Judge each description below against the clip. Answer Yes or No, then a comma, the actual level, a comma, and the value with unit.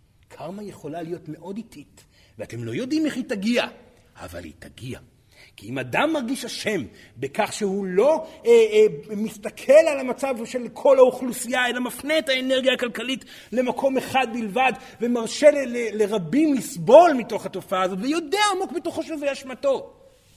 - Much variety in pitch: Yes, wide, 5.8 semitones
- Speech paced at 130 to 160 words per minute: Yes, average, 145 wpm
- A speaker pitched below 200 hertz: No, very high, 250 Hz